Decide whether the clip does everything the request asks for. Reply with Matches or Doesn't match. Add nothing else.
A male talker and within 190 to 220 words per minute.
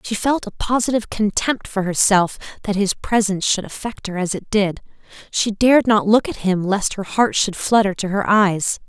Doesn't match